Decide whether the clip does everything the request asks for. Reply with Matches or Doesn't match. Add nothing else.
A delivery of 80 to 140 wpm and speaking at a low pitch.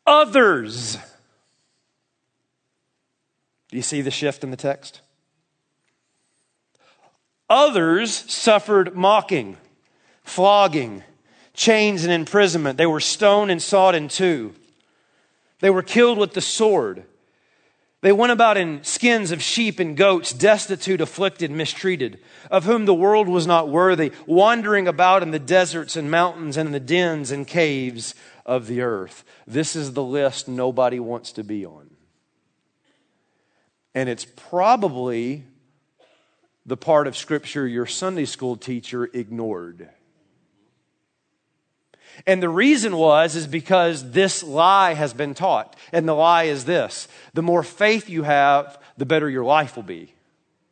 Doesn't match